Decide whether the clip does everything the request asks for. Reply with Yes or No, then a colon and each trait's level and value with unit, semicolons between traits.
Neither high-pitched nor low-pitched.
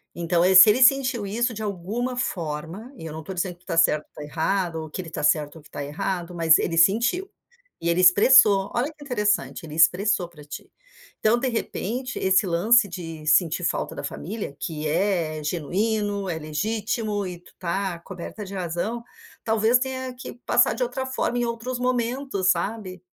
No: high, 195 Hz